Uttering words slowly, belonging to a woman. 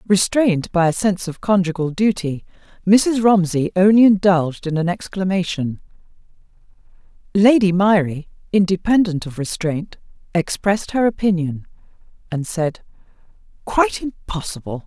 Yes: slow, 105 wpm; female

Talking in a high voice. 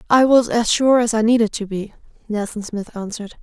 Yes: high, 220 Hz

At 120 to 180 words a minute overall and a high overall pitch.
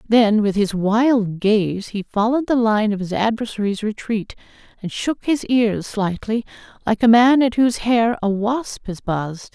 Yes: average, 175 wpm; high, 220 Hz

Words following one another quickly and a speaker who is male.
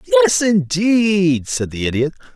No: slow, 125 wpm; male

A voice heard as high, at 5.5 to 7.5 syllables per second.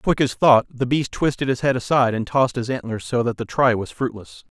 No: low, 125 Hz; 5.7 syllables/s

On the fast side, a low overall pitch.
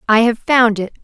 No: fast, 230 wpm; high, 230 Hz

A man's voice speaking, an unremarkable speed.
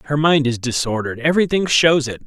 Yes: male; average, 160 wpm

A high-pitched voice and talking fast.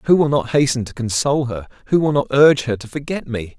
No: low, 135 Hz; fast, 250 wpm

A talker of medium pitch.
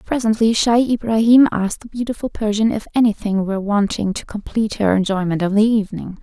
No: high, 215 Hz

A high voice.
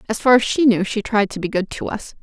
Yes: high, 215 Hz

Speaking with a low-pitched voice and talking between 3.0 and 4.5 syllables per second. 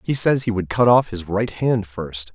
Yes: low, 105 Hz; 4.4 syllables/s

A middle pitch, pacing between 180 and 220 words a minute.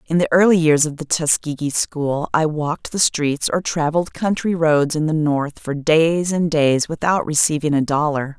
Yes: medium, 155 Hz; average, 195 wpm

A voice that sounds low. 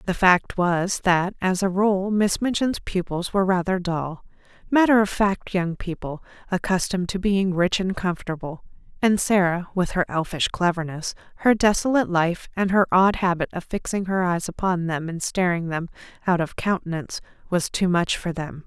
No: medium, 185 Hz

